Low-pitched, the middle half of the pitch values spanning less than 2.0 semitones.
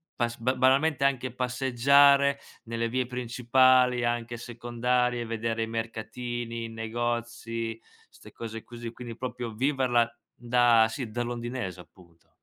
Yes: low, 120 Hz; narrow, 1.6 semitones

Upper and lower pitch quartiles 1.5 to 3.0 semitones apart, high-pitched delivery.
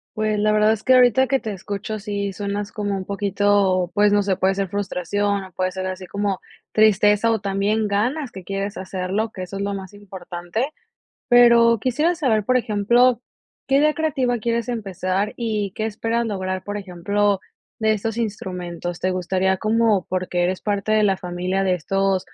Yes: average, 2.7 semitones; high, 205 Hz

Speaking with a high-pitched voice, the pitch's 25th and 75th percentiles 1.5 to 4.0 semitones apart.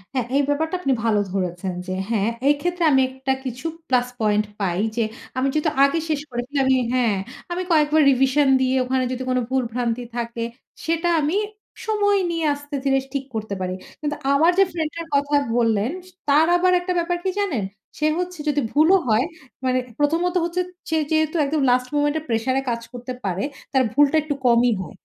No: very high, 275 Hz; average, 4.6 semitones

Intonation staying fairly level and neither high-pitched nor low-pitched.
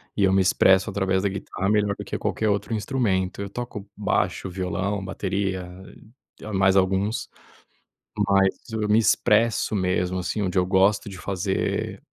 No: narrow, 1.7 semitones; very low, 95 Hz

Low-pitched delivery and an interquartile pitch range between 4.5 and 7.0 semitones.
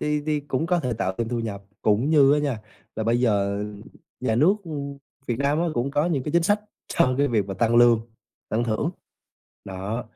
Yes: low, 120 Hz; average, 4.9 semitones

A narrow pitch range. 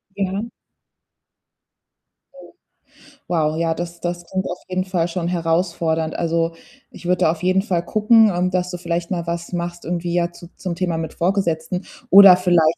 Yes: narrow, 1.6 semitones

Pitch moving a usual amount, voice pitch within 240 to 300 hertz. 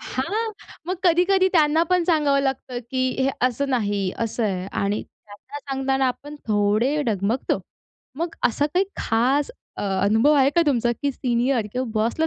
Yes: average, 4.7 semitones; very high, 265 Hz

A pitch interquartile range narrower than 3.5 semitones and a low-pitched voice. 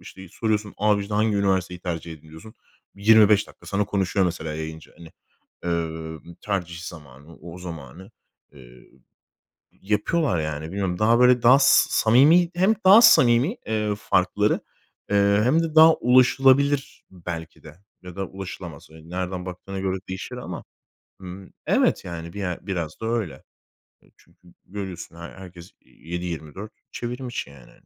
No: average, 4.5 semitones; very low, 95 Hz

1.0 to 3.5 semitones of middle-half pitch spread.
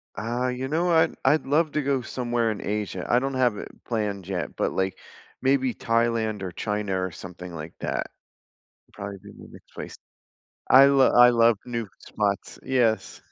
No: average, 4.4 semitones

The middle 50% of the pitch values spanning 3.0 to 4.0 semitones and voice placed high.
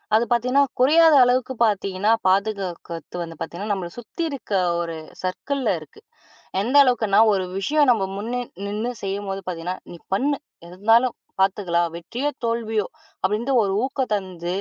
No: average, 4.9 semitones; high, 210 Hz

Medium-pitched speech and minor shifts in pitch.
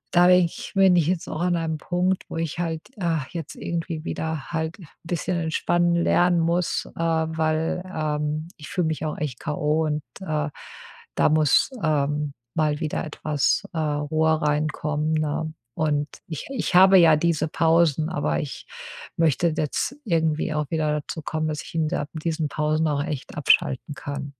Yes: medium, 160 Hz; narrow, 1.9 semitones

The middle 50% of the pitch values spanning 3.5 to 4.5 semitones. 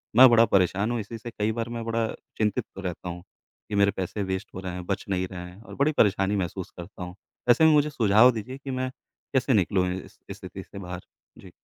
Yes: average, 4.0 semitones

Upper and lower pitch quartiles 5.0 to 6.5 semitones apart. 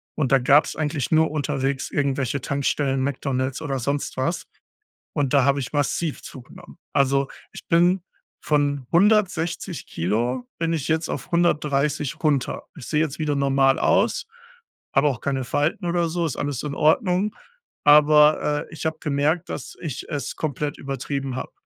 No: narrow, 2.6 semitones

